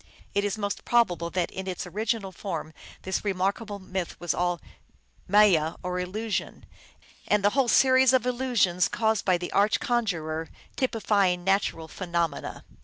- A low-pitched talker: No, high, 195 Hz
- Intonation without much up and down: No, average, 3.7 semitones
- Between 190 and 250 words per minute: No, average, 150 wpm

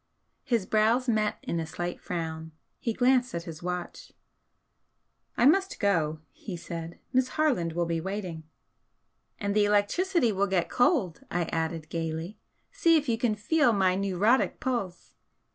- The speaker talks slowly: No, average, 150 wpm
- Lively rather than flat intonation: Yes, wide, 6.1 semitones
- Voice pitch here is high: Yes, high, 200 Hz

